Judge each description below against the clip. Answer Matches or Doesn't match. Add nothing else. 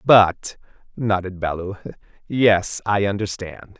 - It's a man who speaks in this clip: Matches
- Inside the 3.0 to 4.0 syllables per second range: Matches